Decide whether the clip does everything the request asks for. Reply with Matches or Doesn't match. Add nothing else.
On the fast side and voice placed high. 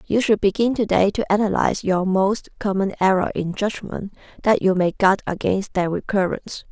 Doesn't match